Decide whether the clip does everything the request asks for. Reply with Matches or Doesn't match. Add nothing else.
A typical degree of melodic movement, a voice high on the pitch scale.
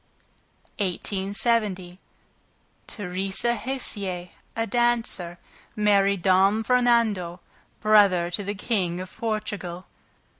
Matches